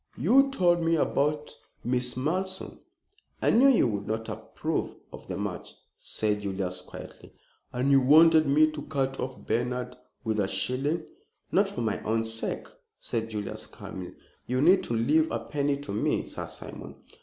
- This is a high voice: No, low, 135 Hz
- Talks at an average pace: Yes, average, 165 wpm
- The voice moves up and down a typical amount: No, wide, 5.9 semitones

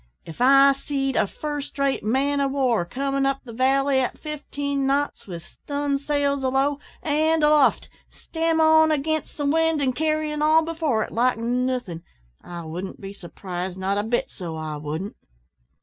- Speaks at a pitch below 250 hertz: No, very high, 275 Hz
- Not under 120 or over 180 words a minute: Yes, average, 165 wpm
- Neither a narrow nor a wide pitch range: Yes, average, 4.8 semitones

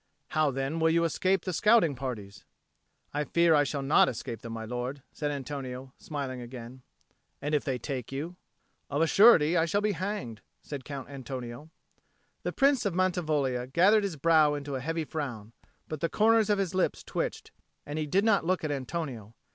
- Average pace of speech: Yes, average, 185 wpm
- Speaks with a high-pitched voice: No, medium, 145 Hz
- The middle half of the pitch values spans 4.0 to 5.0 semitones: Yes, average, 4.6 semitones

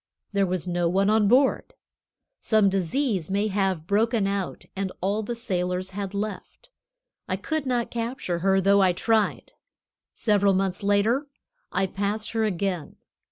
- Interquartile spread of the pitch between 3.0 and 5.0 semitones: No, narrow, 2.6 semitones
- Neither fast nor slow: Yes, average, 150 wpm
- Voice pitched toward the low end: No, high, 200 Hz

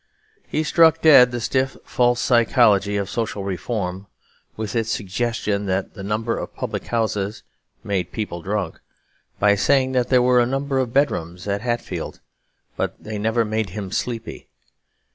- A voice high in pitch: No, low, 110 Hz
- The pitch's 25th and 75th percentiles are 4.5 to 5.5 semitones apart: No, average, 3.5 semitones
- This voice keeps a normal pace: Yes, average, 160 wpm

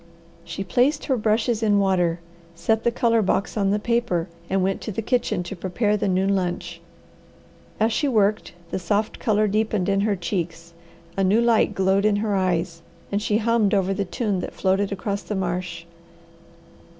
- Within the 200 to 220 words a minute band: No, average, 180 wpm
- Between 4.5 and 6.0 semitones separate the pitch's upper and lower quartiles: No, average, 2.7 semitones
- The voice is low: No, high, 200 Hz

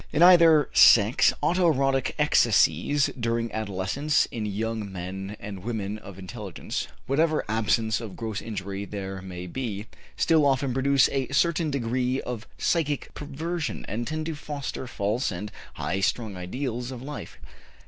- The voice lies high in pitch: No, low, 120 Hz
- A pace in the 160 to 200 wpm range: No, average, 145 wpm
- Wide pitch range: Yes, wide, 5.9 semitones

